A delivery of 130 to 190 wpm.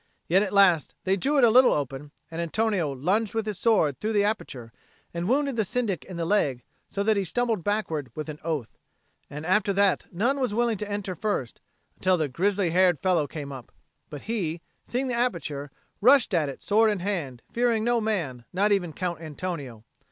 No: average, 200 wpm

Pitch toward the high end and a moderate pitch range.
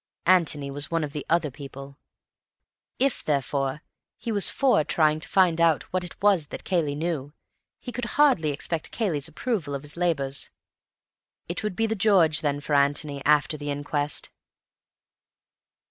No: medium, 155 Hz; average, 4.1 semitones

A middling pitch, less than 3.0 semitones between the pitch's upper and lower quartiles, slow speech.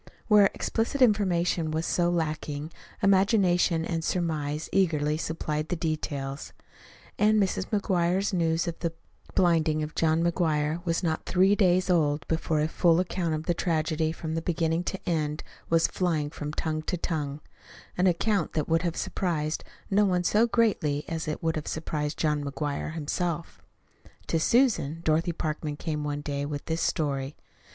No: medium, 165 Hz; narrow, 2.6 semitones; average, 160 wpm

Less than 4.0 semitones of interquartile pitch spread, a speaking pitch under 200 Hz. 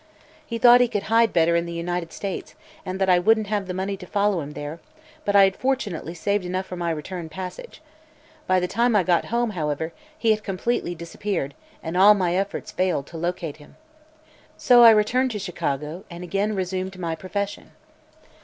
Yes: average, 3.4 semitones; medium, 185 Hz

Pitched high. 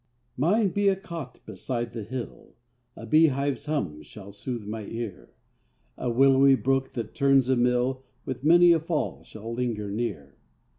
No: low, 125 Hz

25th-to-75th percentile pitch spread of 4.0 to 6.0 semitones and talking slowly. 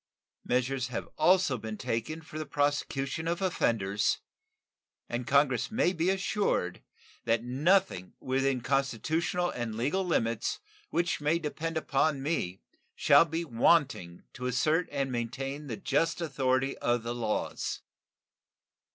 Yes: average, 5.3 semitones; slow, 125 wpm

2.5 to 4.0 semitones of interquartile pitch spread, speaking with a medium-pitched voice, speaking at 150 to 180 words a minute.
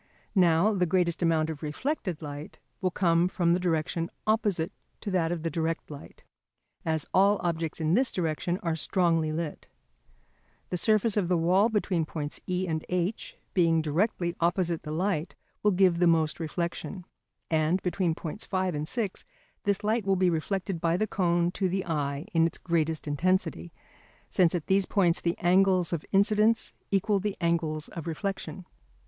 Yes: average, 2.9 semitones; medium, 175 Hz; average, 165 wpm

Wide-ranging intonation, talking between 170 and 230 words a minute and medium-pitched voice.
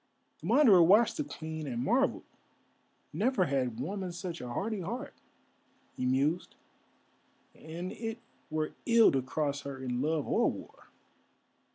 No: wide, 7.5 semitones; average, 140 wpm; medium, 165 Hz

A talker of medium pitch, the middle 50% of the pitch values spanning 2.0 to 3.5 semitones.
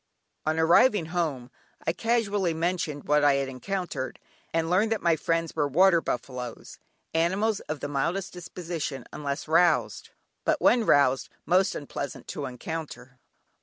No: medium, 165 Hz; average, 4.3 semitones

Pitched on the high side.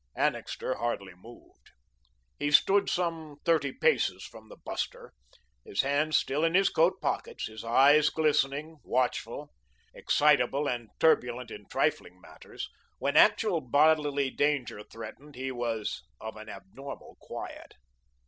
No: medium, 140 Hz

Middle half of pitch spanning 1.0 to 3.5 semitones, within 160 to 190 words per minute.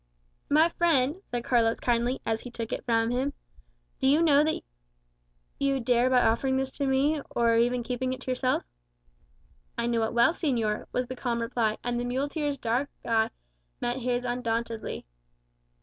Yes: narrow, 2.5 semitones; average, 170 wpm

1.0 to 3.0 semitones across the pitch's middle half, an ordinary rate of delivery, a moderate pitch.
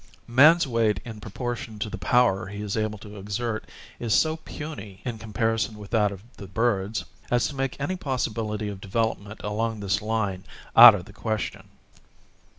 No: narrow, 2.6 semitones; average, 170 wpm; low, 110 Hz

